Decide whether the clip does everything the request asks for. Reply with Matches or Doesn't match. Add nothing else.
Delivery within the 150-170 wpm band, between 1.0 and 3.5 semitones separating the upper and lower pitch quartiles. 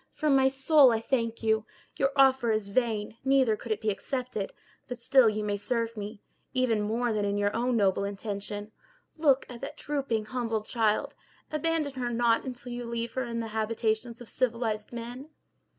Doesn't match